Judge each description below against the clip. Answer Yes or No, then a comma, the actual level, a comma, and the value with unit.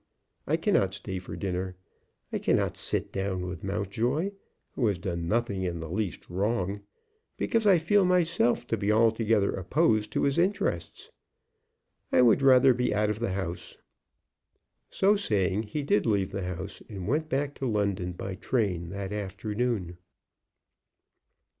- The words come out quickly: No, average, 150 wpm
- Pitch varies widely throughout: No, average, 4.9 semitones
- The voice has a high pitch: No, low, 105 Hz